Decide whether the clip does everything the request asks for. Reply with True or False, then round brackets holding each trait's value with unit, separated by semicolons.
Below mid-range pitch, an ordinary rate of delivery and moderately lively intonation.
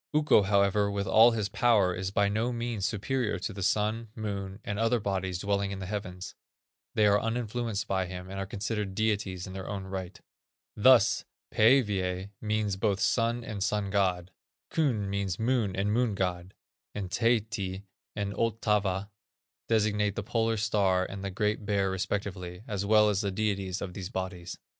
False (100 Hz; 170 wpm; 2.2 semitones)